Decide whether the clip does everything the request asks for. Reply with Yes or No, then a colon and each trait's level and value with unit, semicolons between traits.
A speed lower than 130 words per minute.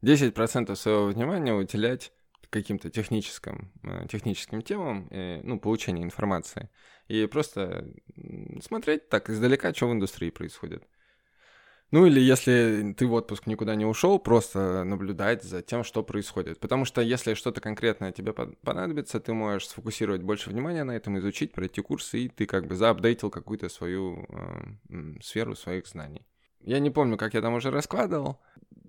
No: average, 150 wpm